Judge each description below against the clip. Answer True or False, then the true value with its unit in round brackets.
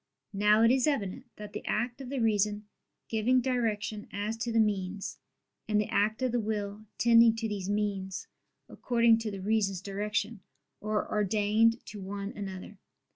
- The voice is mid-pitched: False (210 Hz)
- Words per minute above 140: True (165 wpm)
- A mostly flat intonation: True (2.0 semitones)